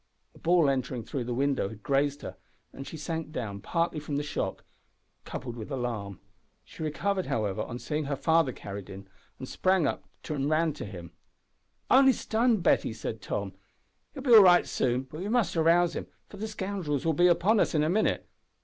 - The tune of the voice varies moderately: No, wide, 6.3 semitones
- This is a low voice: No, medium, 150 Hz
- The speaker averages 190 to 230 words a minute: Yes, average, 195 wpm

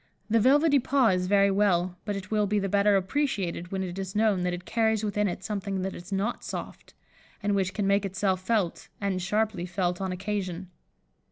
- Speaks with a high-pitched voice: Yes, high, 195 Hz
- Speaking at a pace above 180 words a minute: Yes, average, 200 wpm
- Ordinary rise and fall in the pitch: No, narrow, 2.2 semitones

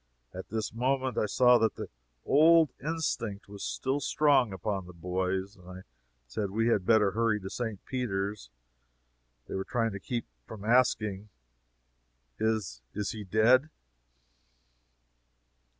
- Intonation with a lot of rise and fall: No, average, 4.2 semitones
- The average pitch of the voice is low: Yes, low, 110 Hz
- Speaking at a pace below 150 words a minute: Yes, slow, 135 wpm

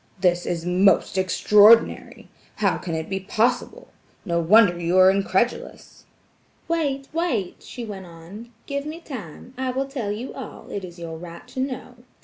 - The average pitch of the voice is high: Yes, high, 205 Hz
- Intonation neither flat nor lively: No, wide, 6.3 semitones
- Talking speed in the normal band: Yes, average, 160 wpm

